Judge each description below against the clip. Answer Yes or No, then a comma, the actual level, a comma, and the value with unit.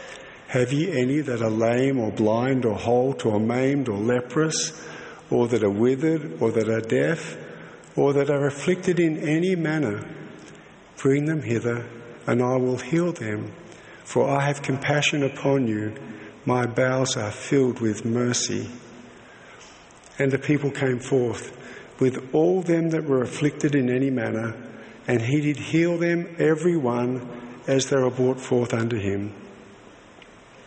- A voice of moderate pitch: No, low, 130 Hz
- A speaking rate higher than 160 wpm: No, average, 150 wpm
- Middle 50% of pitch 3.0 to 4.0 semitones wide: Yes, average, 3.6 semitones